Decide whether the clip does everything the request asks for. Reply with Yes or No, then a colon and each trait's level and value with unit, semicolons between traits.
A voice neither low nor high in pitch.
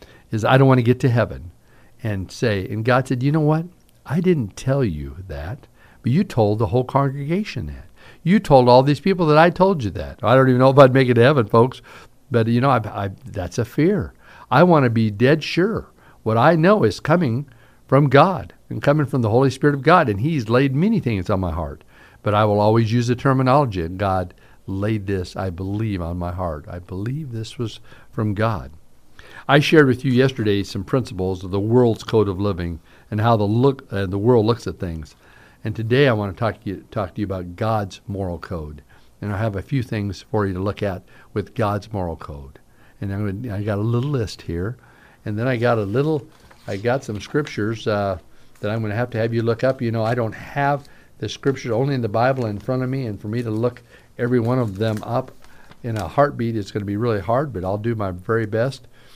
No: low, 115 Hz